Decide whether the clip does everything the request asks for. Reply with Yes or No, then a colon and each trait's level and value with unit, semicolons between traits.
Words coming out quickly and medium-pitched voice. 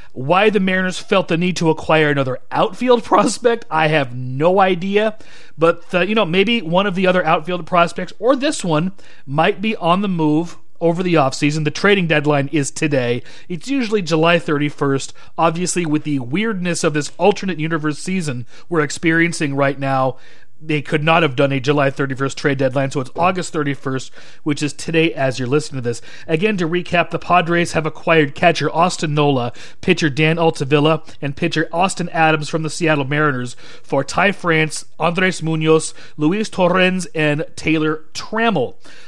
No: average, 170 wpm; medium, 160 Hz